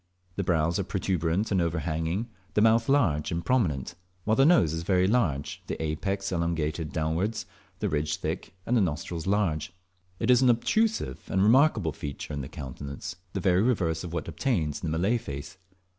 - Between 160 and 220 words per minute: Yes, average, 180 wpm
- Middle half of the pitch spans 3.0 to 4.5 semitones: No, average, 5.2 semitones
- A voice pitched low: Yes, very low, 85 Hz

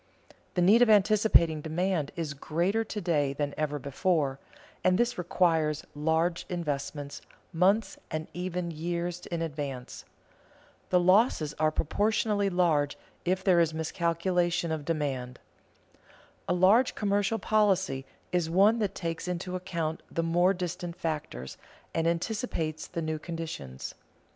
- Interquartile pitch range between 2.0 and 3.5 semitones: Yes, average, 3.2 semitones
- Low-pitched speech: No, medium, 170 Hz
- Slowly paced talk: Yes, slow, 130 wpm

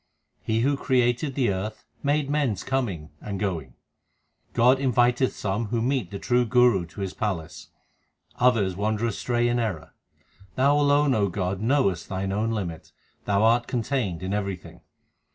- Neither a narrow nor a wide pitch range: Yes, average, 4.4 semitones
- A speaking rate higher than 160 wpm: No, average, 155 wpm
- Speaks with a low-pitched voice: Yes, low, 110 Hz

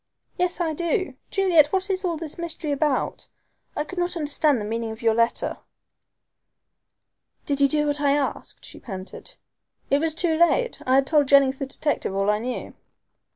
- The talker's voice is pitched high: Yes, very high, 295 Hz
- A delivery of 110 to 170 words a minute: No, average, 180 wpm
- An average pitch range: Yes, average, 4.3 semitones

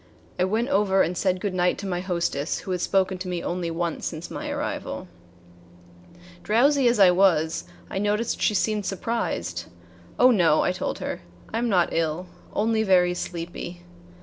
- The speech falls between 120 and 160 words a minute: No, average, 175 wpm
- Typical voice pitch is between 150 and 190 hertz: Yes, medium, 185 Hz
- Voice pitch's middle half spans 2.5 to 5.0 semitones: Yes, average, 3.2 semitones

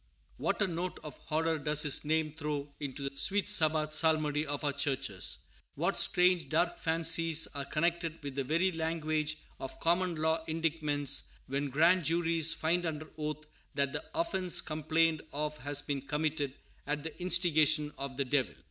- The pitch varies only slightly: Yes, narrow, 2.2 semitones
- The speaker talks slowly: No, average, 165 wpm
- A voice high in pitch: No, medium, 155 Hz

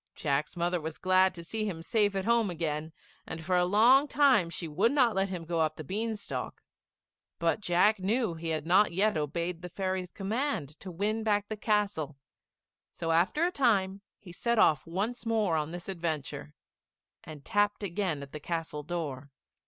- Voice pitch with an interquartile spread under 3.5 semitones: No, average, 4.4 semitones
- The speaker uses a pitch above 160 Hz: Yes, medium, 185 Hz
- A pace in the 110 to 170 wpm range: No, average, 185 wpm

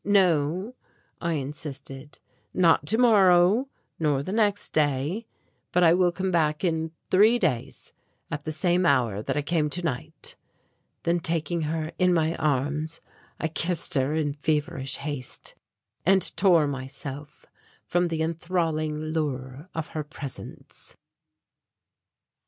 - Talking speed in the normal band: No, slow, 125 wpm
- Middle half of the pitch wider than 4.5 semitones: No, average, 3.2 semitones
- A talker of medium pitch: Yes, medium, 160 Hz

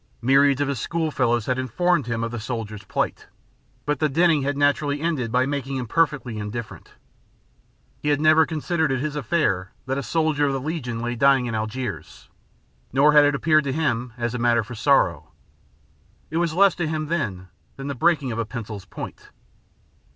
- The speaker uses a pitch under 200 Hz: Yes, low, 135 Hz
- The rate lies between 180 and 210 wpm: Yes, average, 190 wpm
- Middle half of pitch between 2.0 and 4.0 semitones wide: No, average, 4.4 semitones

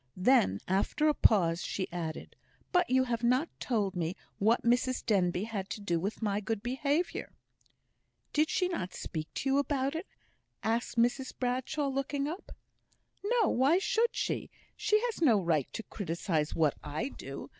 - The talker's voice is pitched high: Yes, high, 235 Hz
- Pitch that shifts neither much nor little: No, wide, 6.9 semitones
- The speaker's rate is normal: Yes, average, 165 wpm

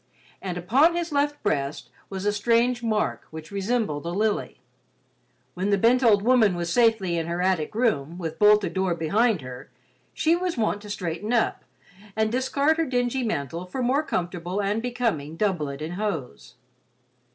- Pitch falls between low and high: No, high, 205 Hz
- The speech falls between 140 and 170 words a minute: Yes, average, 165 wpm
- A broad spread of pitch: Yes, wide, 5.8 semitones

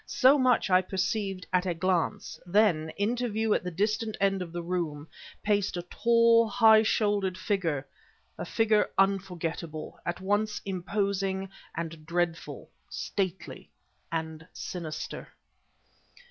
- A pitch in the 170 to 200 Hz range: Yes, high, 190 Hz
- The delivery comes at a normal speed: No, slow, 125 wpm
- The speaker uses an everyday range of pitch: Yes, average, 3.5 semitones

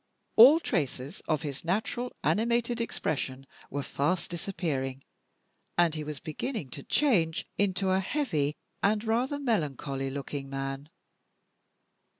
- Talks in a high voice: No, medium, 165 Hz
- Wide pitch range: Yes, wide, 8.0 semitones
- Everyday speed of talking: No, slow, 120 wpm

